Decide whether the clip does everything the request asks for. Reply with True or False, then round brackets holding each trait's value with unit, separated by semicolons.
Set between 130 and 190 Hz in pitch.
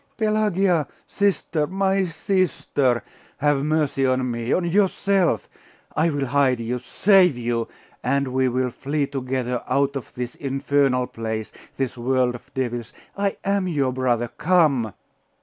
True (135 Hz)